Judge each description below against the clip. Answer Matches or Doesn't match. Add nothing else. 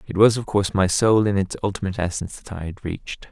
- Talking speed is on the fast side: Matches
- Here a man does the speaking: Matches